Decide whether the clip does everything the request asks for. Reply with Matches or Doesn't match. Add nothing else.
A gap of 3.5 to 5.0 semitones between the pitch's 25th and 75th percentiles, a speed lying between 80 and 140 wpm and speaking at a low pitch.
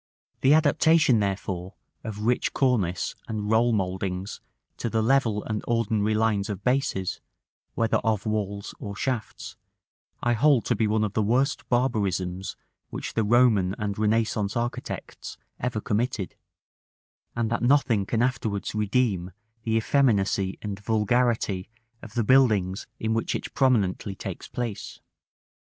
Doesn't match